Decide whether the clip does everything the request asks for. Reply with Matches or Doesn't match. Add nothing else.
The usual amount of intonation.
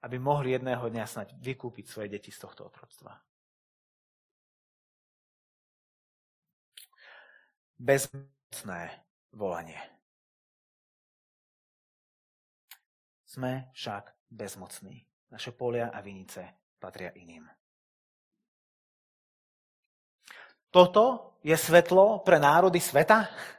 Doesn't match